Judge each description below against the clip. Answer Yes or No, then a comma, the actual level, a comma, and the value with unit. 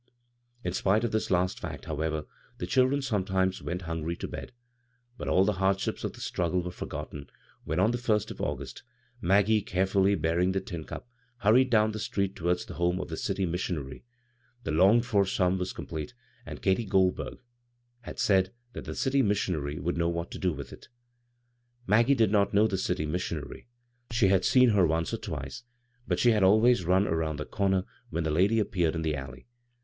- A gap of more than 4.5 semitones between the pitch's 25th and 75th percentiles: No, average, 3.8 semitones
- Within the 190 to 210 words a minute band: Yes, average, 195 wpm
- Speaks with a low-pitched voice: Yes, very low, 95 Hz